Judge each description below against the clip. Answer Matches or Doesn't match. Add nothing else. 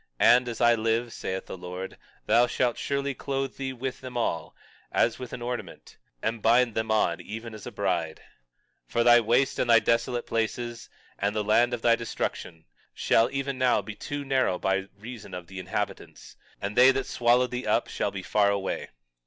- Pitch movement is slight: Doesn't match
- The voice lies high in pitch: Doesn't match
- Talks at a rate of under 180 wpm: Doesn't match